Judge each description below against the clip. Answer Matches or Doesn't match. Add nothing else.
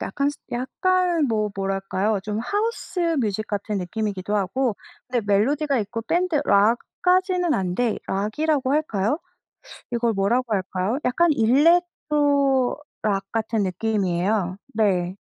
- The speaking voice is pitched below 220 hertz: Doesn't match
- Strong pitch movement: Matches